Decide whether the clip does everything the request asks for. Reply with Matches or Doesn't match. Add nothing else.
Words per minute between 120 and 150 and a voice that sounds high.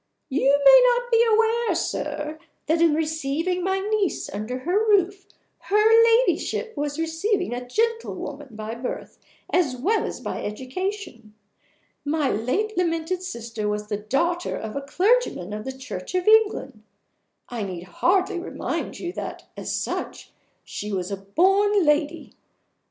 Matches